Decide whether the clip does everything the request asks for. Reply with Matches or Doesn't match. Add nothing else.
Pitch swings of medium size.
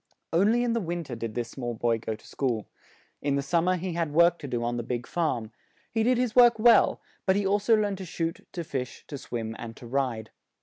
Doesn't match